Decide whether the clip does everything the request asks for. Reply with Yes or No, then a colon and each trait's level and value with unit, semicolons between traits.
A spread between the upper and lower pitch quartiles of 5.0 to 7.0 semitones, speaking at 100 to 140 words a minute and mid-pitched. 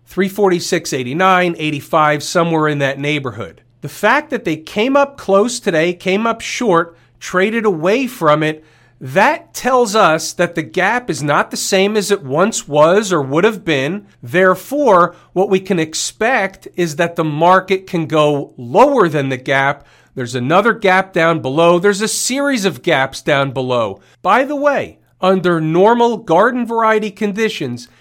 No: wide, 5.6 semitones; average, 160 wpm; medium, 175 Hz